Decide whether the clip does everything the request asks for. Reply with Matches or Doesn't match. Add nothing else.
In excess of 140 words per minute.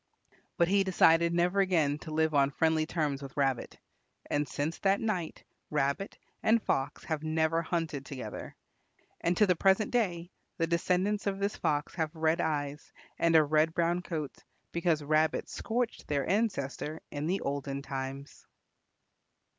Matches